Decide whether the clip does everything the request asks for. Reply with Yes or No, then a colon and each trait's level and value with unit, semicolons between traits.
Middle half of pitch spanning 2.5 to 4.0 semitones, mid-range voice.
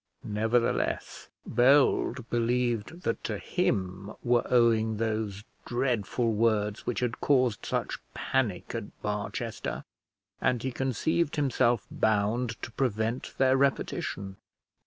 No: average, 2.9 semitones; low, 115 Hz